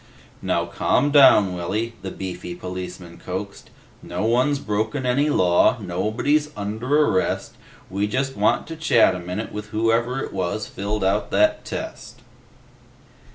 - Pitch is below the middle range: Yes, low, 105 Hz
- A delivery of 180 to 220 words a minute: No, average, 140 wpm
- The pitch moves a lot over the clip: Yes, wide, 5.8 semitones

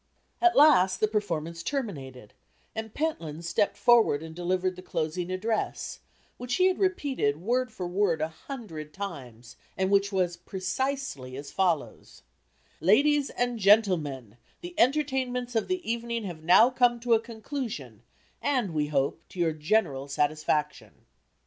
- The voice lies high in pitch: Yes, high, 195 Hz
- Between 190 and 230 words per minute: No, average, 145 wpm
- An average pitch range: No, wide, 7.2 semitones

